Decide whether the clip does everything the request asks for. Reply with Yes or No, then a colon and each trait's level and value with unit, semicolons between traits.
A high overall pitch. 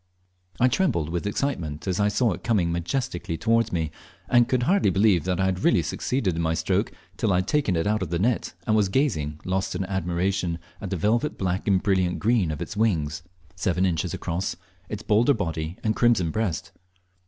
No: very low, 95 Hz